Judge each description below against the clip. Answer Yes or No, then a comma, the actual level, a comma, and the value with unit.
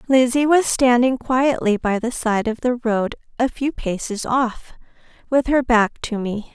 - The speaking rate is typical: Yes, average, 175 wpm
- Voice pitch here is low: No, high, 240 Hz